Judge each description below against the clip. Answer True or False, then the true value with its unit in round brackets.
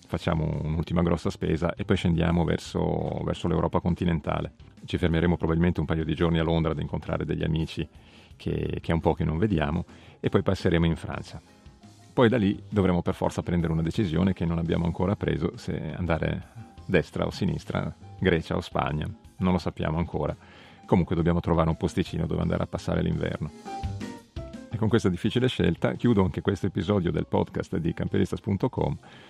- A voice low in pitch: True (85 Hz)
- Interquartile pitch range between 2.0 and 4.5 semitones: True (2.9 semitones)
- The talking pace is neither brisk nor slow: False (175 wpm)